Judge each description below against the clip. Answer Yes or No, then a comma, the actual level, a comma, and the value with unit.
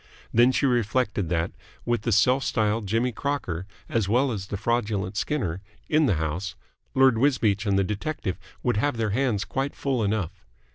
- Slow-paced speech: No, average, 175 wpm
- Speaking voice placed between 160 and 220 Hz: No, low, 110 Hz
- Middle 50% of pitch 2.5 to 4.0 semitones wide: No, average, 4.5 semitones